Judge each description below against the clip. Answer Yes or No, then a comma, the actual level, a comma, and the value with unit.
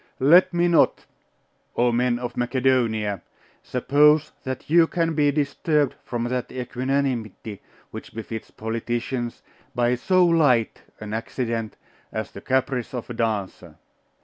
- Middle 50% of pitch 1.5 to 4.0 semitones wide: Yes, average, 3.7 semitones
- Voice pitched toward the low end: Yes, low, 125 Hz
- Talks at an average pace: No, slow, 125 wpm